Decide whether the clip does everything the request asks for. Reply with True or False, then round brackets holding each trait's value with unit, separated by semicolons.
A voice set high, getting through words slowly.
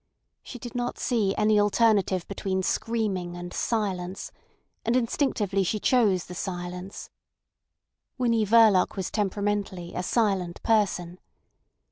True (200 Hz; 115 wpm)